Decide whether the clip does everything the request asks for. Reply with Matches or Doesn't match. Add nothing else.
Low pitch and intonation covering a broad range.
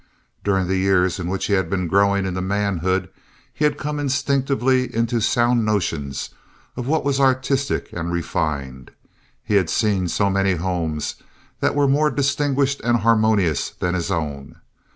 Matches